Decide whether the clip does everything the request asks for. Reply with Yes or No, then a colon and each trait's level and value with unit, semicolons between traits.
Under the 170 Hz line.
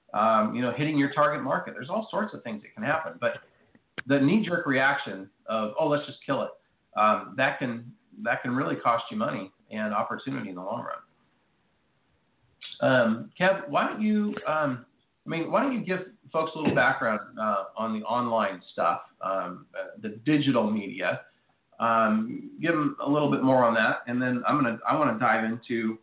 Yes: low, 135 Hz